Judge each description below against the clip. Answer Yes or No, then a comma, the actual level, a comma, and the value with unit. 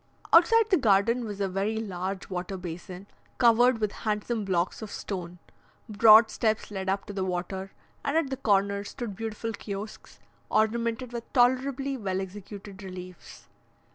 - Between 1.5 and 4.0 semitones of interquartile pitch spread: Yes, average, 3.4 semitones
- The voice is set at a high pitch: Yes, high, 210 Hz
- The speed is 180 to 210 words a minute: No, average, 150 wpm